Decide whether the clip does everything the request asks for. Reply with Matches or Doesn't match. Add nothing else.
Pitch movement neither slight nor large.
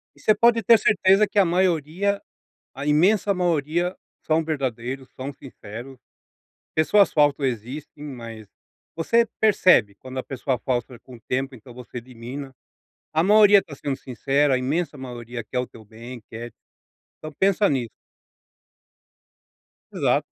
Doesn't match